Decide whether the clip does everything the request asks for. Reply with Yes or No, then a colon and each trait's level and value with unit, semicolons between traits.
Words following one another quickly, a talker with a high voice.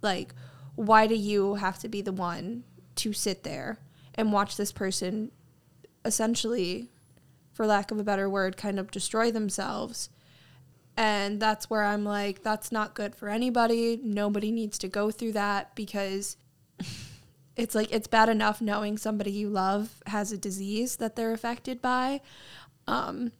No: average, 155 wpm; high, 205 Hz